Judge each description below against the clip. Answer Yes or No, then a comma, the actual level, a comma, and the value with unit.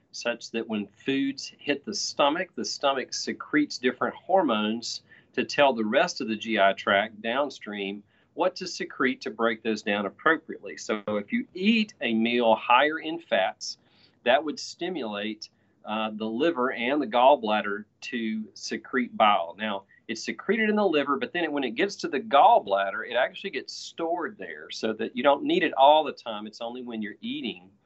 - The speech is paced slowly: No, average, 180 wpm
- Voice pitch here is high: No, low, 115 Hz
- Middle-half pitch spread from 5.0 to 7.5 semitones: Yes, average, 5.3 semitones